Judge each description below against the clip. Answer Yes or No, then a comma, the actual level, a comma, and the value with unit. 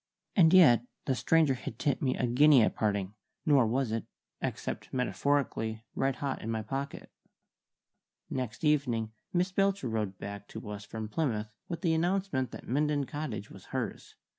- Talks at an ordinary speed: Yes, average, 165 wpm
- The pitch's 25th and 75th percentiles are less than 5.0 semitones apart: No, average, 5.3 semitones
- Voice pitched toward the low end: Yes, low, 130 Hz